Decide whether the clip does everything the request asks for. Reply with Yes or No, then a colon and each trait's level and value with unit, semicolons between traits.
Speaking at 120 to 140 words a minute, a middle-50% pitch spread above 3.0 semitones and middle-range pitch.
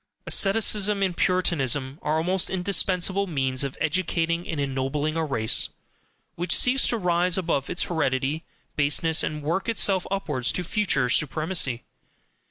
Yes: slow, 135 wpm; average, 4.7 semitones; medium, 165 Hz